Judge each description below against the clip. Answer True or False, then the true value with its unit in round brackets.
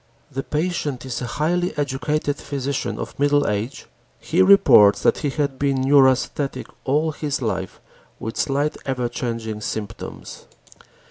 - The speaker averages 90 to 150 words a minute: True (135 wpm)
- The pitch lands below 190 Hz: True (135 Hz)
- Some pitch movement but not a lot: True (3.2 semitones)